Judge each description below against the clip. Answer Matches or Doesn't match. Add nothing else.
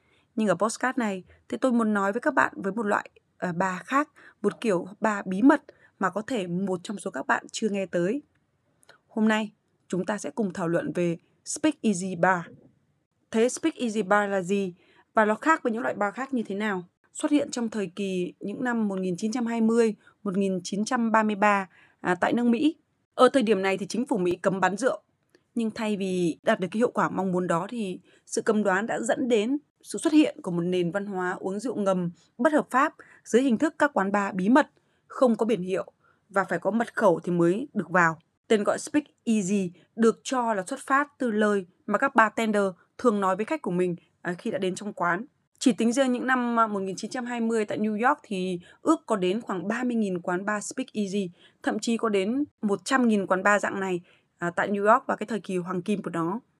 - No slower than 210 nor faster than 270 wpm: Matches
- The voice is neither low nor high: Doesn't match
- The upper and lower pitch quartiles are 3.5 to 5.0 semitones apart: Matches